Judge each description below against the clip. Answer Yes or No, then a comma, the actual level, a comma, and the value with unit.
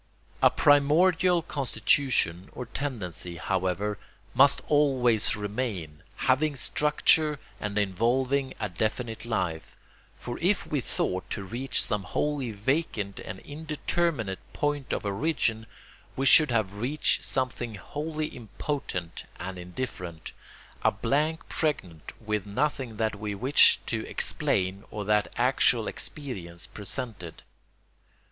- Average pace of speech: No, slow, 115 wpm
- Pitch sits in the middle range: No, low, 115 Hz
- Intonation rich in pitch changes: Yes, wide, 6.4 semitones